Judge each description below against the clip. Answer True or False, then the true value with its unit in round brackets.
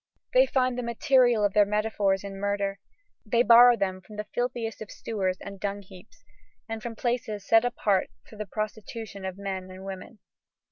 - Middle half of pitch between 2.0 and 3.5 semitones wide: True (2.9 semitones)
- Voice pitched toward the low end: False (210 Hz)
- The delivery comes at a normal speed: True (175 wpm)